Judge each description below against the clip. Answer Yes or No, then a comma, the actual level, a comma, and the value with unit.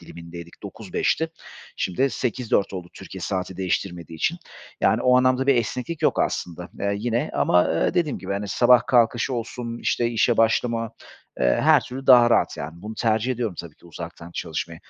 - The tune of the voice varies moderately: No, wide, 5.9 semitones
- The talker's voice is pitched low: Yes, low, 115 Hz